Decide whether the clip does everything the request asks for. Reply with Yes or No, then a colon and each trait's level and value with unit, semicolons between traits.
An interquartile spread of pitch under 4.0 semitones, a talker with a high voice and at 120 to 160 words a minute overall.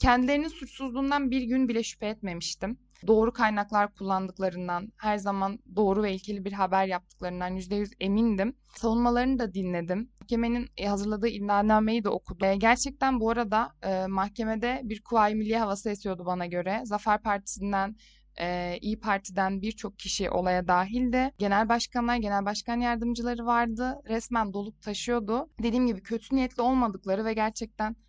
Yes: average, 3.3 semitones; high, 215 Hz; fast, 140 wpm